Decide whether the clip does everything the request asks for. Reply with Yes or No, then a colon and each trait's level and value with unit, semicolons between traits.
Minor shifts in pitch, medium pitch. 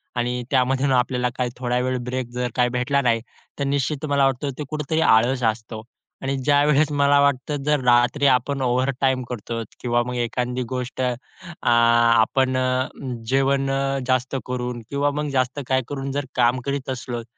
No: narrow, 2.1 semitones; low, 130 Hz